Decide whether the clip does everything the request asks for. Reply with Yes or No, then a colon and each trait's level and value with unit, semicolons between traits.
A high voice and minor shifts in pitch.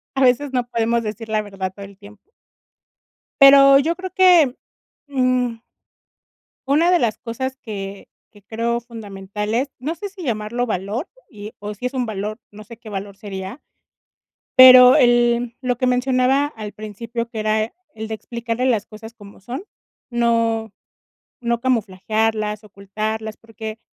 No: high, 230 Hz; average, 3.1 semitones